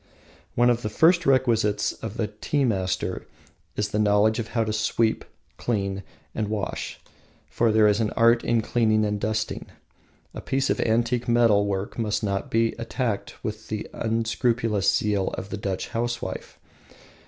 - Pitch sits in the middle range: No, low, 110 Hz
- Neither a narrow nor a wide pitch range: No, narrow, 2.1 semitones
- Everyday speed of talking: Yes, average, 160 wpm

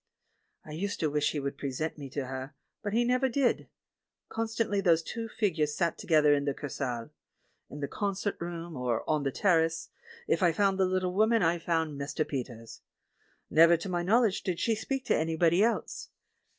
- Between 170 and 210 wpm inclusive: Yes, average, 185 wpm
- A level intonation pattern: No, wide, 5.6 semitones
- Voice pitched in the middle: Yes, medium, 165 Hz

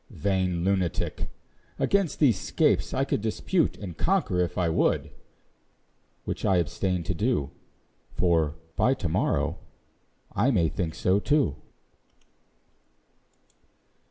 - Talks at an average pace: No, slow, 115 wpm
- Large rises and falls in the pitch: No, average, 5.0 semitones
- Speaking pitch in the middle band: No, very low, 95 Hz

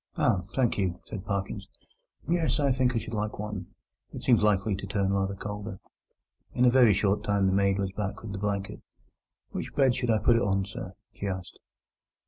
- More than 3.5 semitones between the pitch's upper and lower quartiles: No, average, 2.8 semitones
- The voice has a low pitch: Yes, low, 105 Hz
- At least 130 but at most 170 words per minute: No, average, 200 wpm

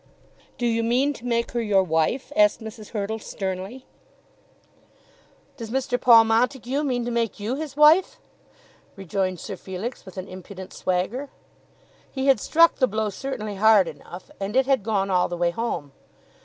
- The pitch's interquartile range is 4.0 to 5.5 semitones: Yes, average, 5.0 semitones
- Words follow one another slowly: No, average, 165 wpm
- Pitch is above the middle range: Yes, high, 225 Hz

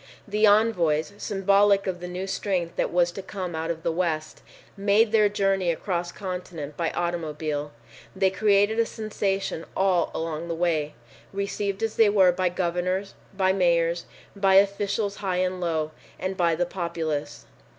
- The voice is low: No, medium, 185 Hz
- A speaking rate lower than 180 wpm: Yes, average, 160 wpm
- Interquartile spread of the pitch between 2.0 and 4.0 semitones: Yes, average, 2.8 semitones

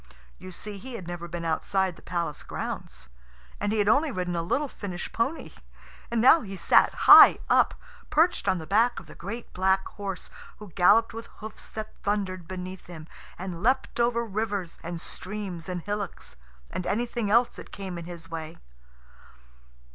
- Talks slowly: No, average, 175 wpm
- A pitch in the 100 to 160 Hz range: No, high, 195 Hz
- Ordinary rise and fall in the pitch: Yes, average, 4.0 semitones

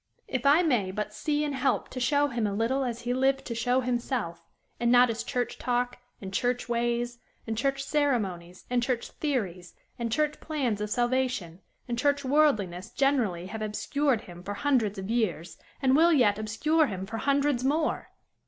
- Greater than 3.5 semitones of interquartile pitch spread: Yes, average, 4.5 semitones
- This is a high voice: Yes, high, 245 Hz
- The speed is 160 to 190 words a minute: Yes, average, 180 wpm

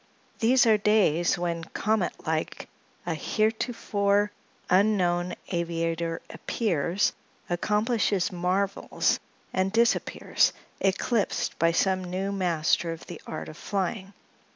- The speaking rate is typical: No, slow, 105 wpm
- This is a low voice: No, high, 190 Hz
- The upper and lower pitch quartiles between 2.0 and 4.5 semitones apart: Yes, average, 3.5 semitones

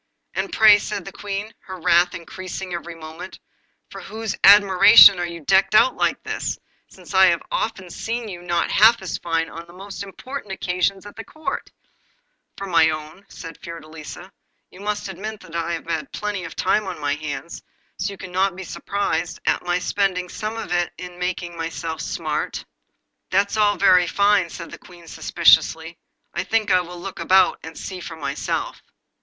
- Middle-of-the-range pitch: Yes, medium, 180 Hz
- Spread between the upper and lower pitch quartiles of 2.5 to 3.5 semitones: Yes, average, 3.0 semitones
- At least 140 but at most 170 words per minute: No, average, 180 wpm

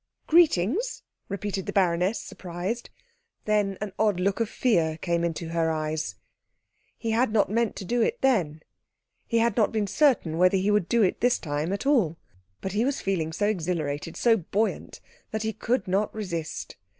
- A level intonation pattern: No, average, 4.9 semitones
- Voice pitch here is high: Yes, high, 200 Hz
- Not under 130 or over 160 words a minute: No, average, 175 wpm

